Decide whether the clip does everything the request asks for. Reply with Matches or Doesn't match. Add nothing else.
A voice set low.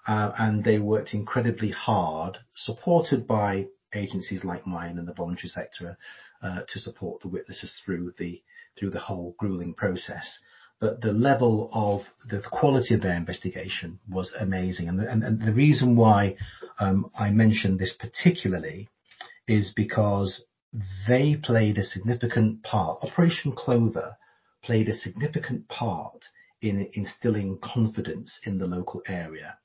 Matches